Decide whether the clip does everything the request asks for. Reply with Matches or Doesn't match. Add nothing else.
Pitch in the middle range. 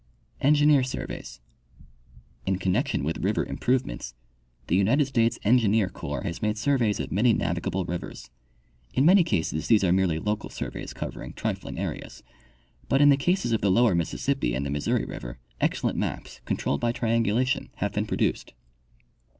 Doesn't match